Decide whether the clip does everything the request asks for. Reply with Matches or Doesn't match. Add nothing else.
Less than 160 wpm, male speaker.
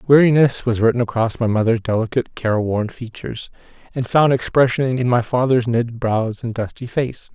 Doesn't match